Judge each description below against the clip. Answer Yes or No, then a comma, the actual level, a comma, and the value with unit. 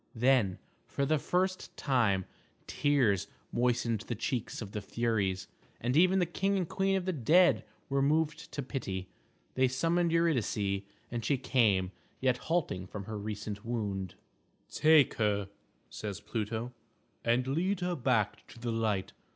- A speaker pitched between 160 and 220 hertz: No, low, 120 Hz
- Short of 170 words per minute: Yes, average, 150 wpm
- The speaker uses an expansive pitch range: Yes, wide, 6.8 semitones